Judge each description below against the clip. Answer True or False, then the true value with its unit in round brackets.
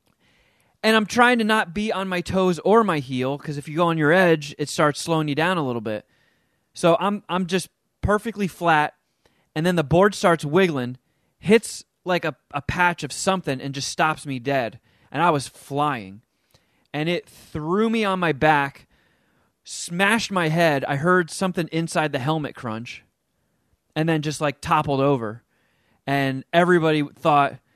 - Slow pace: False (175 wpm)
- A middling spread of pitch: True (4.4 semitones)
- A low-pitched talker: False (160 Hz)